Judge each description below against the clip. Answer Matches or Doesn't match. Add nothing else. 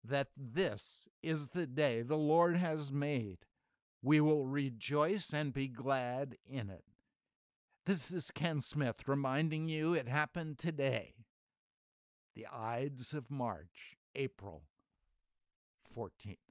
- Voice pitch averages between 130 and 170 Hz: Matches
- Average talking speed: Doesn't match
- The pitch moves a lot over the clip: Doesn't match